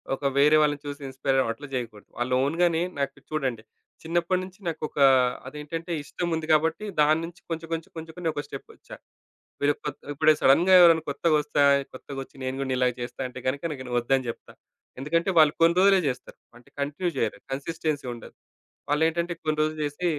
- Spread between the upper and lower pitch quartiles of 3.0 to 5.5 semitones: Yes, average, 3.4 semitones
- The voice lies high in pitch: No, medium, 150 Hz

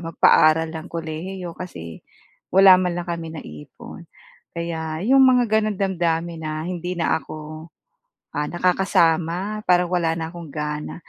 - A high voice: No, medium, 170 Hz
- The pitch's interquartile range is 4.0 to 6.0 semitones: No, narrow, 2.4 semitones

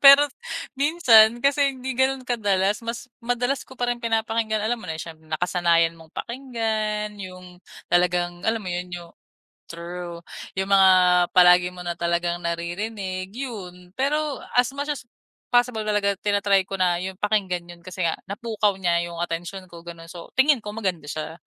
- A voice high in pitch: Yes, high, 195 Hz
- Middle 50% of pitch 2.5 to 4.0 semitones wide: No, average, 5.1 semitones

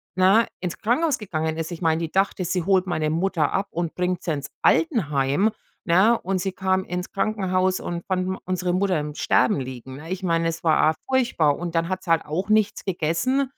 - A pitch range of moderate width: Yes, average, 3.1 semitones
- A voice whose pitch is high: No, medium, 180 Hz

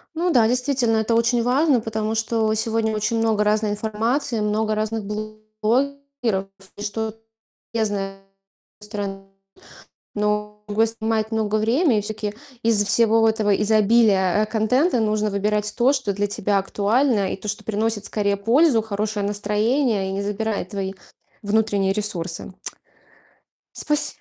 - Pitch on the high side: Yes, high, 215 Hz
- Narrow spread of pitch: Yes, narrow, 1.7 semitones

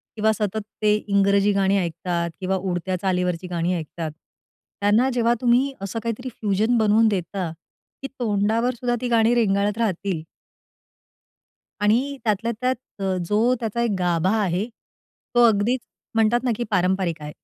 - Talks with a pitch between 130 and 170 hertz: No, high, 205 Hz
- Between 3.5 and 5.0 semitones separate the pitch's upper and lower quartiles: Yes, average, 3.8 semitones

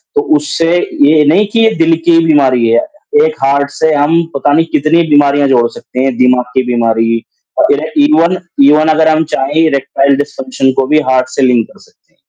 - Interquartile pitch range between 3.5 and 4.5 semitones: Yes, average, 3.8 semitones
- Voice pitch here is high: No, medium, 145 Hz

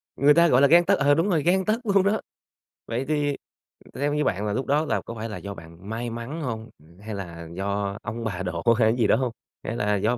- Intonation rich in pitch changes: Yes, wide, 6.6 semitones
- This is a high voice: No, low, 115 Hz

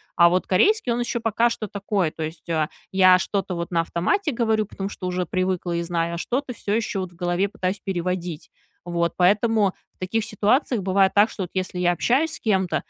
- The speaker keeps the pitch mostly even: No, average, 3.7 semitones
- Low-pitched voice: No, high, 190 Hz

